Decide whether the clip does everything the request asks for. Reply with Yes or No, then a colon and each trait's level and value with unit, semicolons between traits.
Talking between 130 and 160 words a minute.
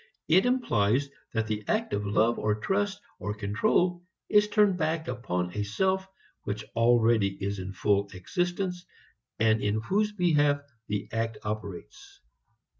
Yes: average, 140 wpm